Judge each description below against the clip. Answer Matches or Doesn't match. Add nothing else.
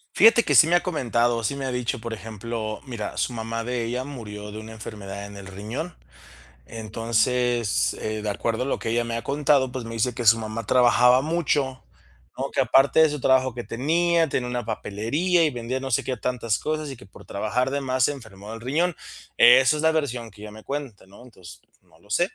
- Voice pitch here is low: Matches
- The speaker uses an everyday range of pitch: Matches